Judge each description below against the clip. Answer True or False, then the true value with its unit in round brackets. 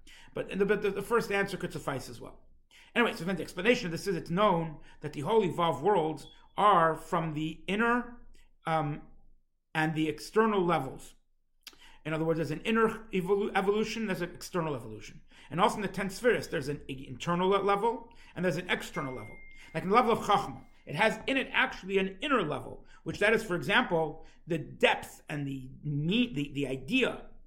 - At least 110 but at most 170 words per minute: False (195 wpm)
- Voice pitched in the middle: True (175 Hz)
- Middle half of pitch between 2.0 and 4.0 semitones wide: False (4.8 semitones)